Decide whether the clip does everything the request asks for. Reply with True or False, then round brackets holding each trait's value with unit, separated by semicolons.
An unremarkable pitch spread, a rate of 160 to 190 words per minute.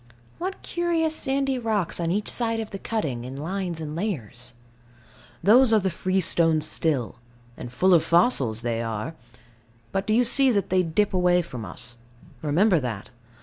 False (7.5 semitones; 165 wpm)